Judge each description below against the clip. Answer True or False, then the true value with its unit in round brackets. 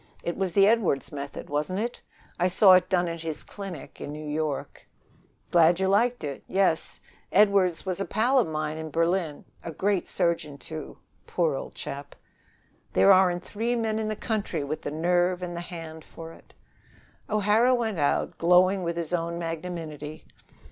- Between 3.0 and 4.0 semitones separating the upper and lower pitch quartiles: True (3.7 semitones)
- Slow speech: False (175 wpm)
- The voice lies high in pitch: False (175 Hz)